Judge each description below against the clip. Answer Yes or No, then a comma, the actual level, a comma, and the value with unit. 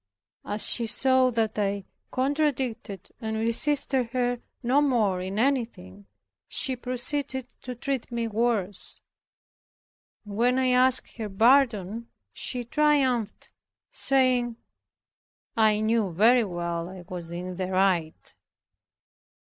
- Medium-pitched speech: No, high, 230 Hz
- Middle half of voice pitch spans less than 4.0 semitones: No, average, 4.4 semitones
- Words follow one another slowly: Yes, slow, 115 wpm